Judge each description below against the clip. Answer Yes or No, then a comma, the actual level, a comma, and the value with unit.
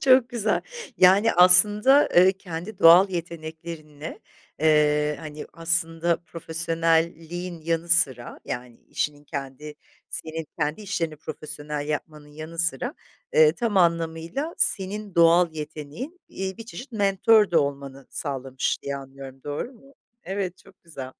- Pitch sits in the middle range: Yes, medium, 165 Hz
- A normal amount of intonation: Yes, average, 4.1 semitones